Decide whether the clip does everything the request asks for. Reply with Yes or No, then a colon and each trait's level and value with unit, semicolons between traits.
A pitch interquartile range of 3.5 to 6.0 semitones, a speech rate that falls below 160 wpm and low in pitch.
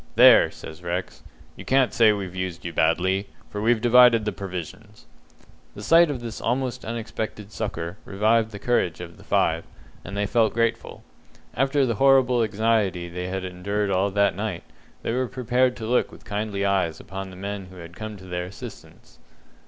No: average, 3.9 semitones; average, 180 wpm; low, 105 Hz